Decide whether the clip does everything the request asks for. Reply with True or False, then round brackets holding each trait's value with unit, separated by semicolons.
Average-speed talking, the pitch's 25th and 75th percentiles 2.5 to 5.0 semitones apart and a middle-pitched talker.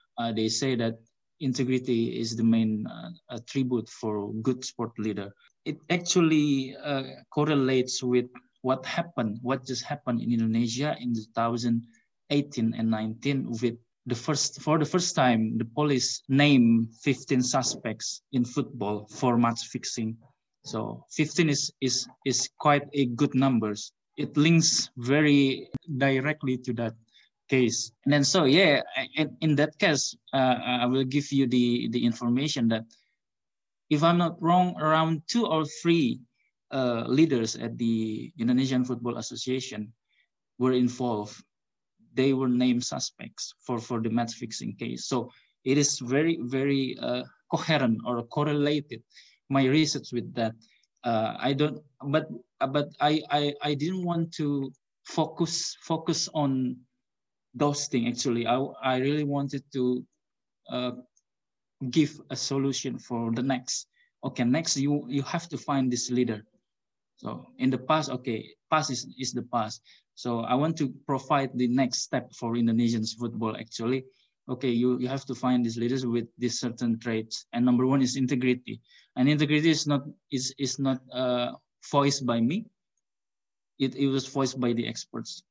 False (150 wpm; 3.4 semitones; 130 Hz)